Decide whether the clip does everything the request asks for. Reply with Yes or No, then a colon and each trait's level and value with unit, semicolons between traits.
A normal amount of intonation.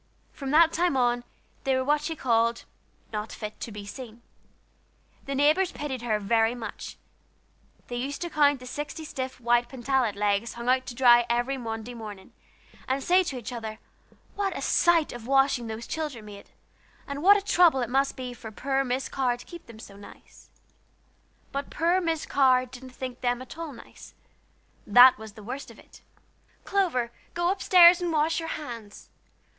Yes: average, 4.1 semitones